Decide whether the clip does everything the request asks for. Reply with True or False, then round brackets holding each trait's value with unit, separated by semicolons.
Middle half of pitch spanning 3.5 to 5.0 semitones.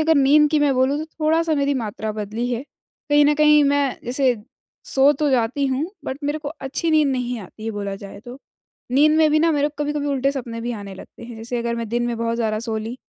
True (4.2 semitones)